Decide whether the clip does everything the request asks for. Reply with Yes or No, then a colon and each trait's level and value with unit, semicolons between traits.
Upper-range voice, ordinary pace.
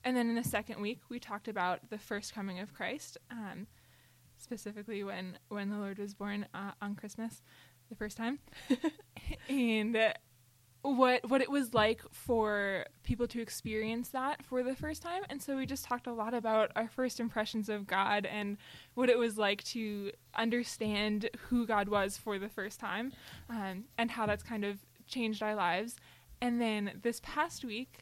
Yes: high, 220 Hz; average, 180 wpm